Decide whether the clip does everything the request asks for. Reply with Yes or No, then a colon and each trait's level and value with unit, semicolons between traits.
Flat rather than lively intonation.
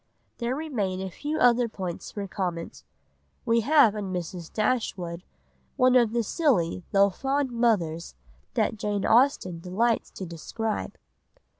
No: average, 5.0 semitones